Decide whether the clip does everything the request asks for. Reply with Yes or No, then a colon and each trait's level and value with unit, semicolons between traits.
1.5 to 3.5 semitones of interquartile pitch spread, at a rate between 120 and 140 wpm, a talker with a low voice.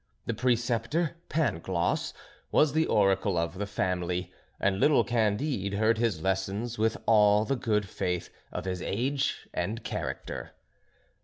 No: average, 3.9 semitones; slow, 135 wpm; low, 105 Hz